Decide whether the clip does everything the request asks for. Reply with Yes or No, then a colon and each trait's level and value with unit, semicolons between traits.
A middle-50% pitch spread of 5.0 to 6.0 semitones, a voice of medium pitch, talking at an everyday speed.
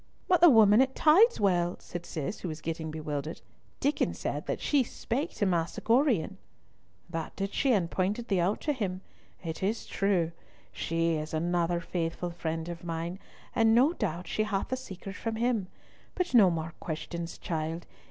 Yes: average, 5.3 semitones; medium, 180 Hz; average, 170 wpm